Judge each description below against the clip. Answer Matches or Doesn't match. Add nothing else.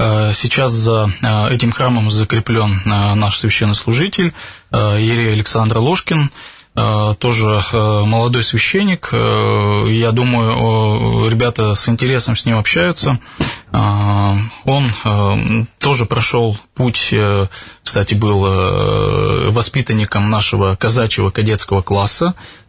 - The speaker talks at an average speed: Doesn't match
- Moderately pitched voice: Doesn't match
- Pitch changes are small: Matches